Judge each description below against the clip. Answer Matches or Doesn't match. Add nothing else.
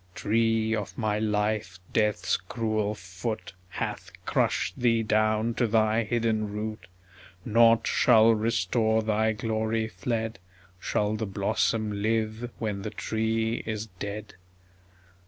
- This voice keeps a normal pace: Doesn't match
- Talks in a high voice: Doesn't match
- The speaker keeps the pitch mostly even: Matches